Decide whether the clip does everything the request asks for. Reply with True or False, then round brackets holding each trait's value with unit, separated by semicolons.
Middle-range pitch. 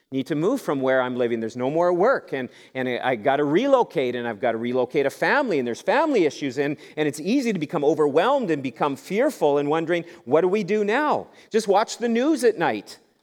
True (150 Hz)